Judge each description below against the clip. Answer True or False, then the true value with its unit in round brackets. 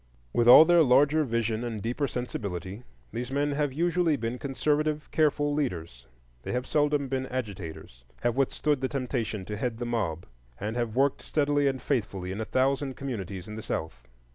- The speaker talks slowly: False (175 wpm)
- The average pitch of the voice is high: False (125 Hz)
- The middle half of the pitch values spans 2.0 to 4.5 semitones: False (5.1 semitones)